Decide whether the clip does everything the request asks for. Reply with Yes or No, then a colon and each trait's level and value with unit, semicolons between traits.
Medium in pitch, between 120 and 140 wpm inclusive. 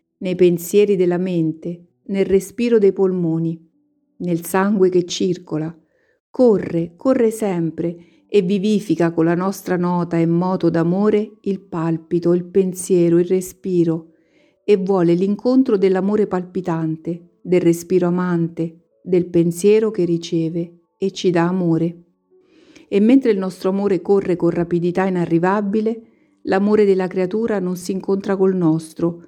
Yes: medium, 180 Hz; average, 130 wpm